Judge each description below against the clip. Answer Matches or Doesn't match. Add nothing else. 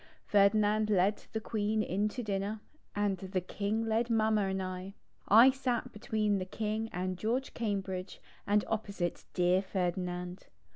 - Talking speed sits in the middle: Matches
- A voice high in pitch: Matches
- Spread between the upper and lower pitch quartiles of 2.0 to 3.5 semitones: Matches